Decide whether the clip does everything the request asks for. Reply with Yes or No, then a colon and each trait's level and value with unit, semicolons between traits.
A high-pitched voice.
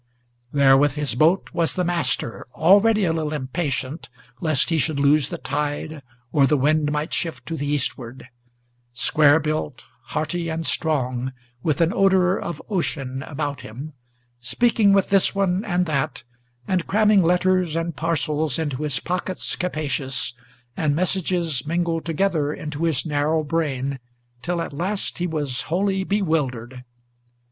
No: medium, 155 Hz